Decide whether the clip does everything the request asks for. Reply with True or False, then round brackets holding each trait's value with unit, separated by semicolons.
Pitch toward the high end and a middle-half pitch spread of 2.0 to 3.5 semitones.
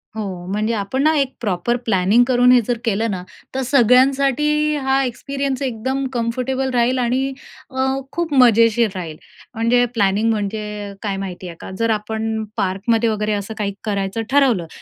False (230 Hz; 4.1 semitones)